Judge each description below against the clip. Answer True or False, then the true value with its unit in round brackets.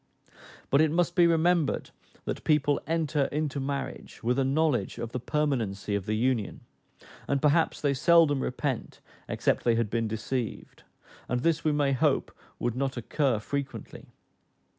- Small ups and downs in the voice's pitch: False (4.0 semitones)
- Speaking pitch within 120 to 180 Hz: True (140 Hz)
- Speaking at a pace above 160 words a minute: False (155 wpm)